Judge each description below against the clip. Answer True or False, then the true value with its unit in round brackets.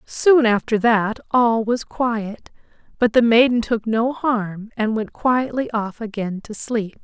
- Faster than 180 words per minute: False (160 wpm)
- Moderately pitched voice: False (225 Hz)